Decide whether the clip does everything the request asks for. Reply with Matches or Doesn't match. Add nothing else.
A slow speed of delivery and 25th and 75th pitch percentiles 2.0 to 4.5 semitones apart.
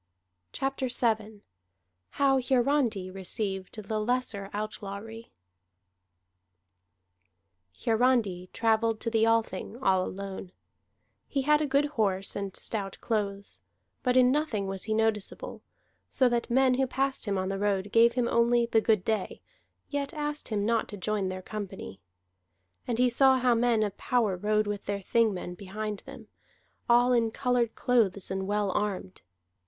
Doesn't match